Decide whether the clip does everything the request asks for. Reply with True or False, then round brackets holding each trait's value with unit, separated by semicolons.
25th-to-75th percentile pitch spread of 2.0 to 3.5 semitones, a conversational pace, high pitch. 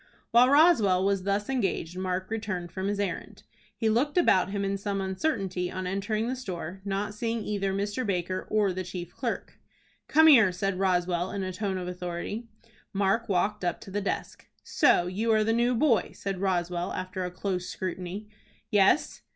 True (2.8 semitones; 180 wpm; 195 Hz)